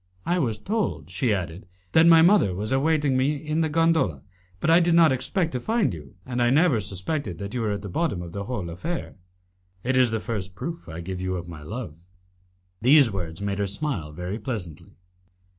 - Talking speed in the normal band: No, fast, 210 wpm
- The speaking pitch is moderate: No, low, 115 Hz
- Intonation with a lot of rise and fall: Yes, wide, 9.0 semitones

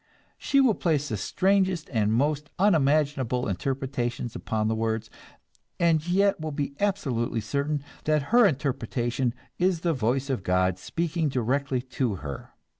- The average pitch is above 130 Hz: Yes, medium, 140 Hz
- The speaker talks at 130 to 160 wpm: Yes, average, 140 wpm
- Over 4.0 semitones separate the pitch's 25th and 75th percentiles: Yes, wide, 5.4 semitones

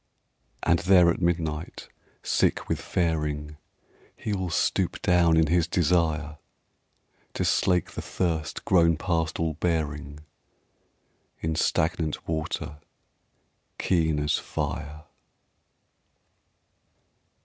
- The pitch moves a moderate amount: No, narrow, 2.2 semitones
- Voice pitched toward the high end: No, very low, 80 Hz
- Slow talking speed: Yes, slow, 95 wpm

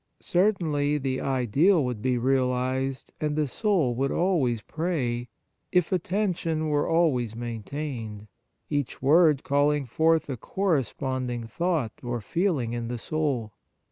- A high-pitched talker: No, medium, 140 Hz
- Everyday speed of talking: No, slow, 130 wpm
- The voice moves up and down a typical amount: Yes, average, 4.8 semitones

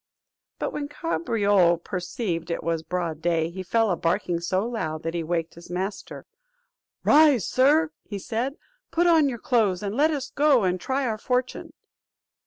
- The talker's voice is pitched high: Yes, high, 200 Hz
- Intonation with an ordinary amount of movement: No, wide, 7.3 semitones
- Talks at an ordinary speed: Yes, average, 170 wpm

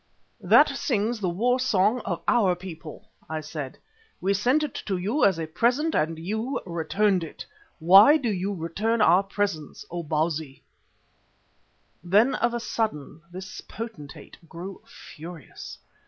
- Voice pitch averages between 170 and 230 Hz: Yes, high, 190 Hz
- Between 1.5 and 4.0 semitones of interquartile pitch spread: No, wide, 5.4 semitones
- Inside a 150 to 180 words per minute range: No, average, 140 wpm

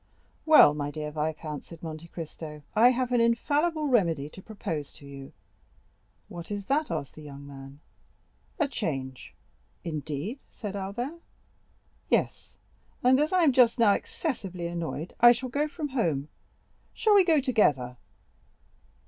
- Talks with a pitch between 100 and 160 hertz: No, high, 190 Hz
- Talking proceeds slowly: No, average, 145 wpm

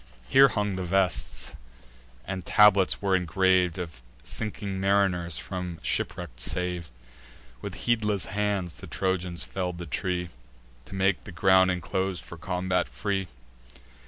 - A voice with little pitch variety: Yes, narrow, 1.6 semitones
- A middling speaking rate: No, slow, 130 wpm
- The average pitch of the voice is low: Yes, very low, 95 Hz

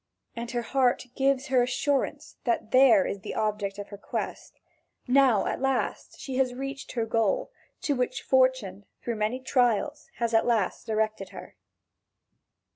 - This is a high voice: Yes, high, 245 Hz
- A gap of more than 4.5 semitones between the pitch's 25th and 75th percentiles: No, average, 3.5 semitones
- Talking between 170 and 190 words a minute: No, average, 155 wpm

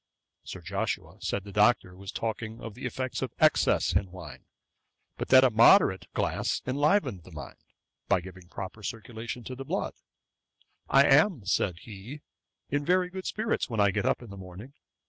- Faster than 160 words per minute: Yes, average, 180 wpm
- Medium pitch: No, low, 115 Hz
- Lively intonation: Yes, wide, 5.8 semitones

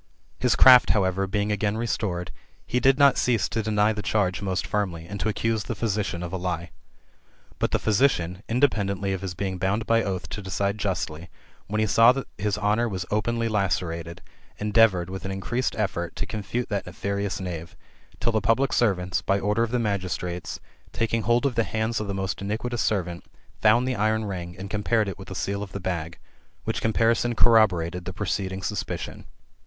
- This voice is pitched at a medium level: No, low, 100 Hz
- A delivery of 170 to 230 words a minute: Yes, average, 190 wpm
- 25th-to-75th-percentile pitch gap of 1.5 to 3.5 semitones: Yes, average, 3.1 semitones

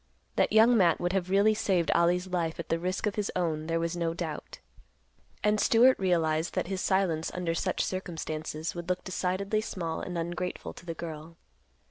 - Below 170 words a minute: No, average, 185 wpm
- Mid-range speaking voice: Yes, medium, 175 Hz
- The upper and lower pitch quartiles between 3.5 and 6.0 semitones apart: No, narrow, 2.4 semitones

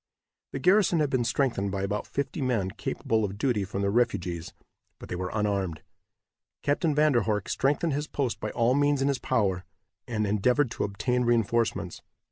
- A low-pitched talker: Yes, low, 115 Hz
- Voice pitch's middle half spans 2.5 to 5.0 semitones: No, wide, 5.6 semitones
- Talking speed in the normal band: Yes, average, 180 wpm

